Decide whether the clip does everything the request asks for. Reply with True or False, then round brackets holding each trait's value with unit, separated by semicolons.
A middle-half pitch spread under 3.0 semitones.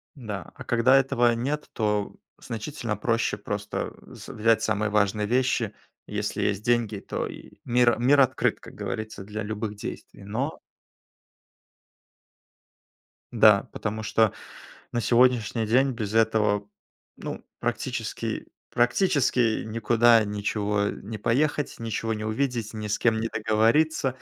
True (2.4 semitones)